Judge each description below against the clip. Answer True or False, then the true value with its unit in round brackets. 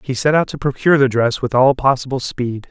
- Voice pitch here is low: True (130 Hz)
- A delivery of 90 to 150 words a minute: False (245 wpm)